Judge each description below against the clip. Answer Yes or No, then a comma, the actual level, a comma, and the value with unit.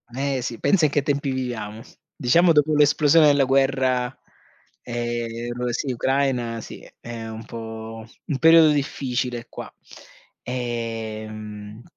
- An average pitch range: Yes, average, 3.5 semitones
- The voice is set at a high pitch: No, low, 125 Hz